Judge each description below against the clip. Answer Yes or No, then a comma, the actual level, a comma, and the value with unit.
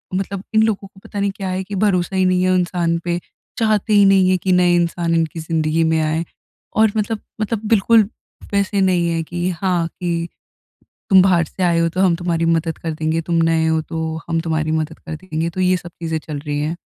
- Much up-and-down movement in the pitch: No, average, 2.7 semitones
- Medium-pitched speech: Yes, medium, 175 Hz